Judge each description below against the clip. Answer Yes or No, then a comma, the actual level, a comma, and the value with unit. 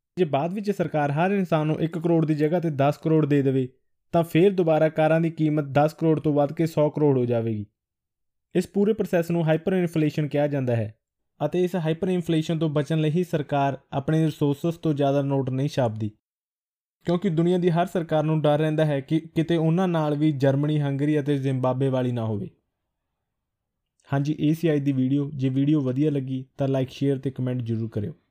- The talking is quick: Yes, fast, 195 wpm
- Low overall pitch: No, medium, 150 Hz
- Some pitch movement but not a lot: Yes, average, 3.1 semitones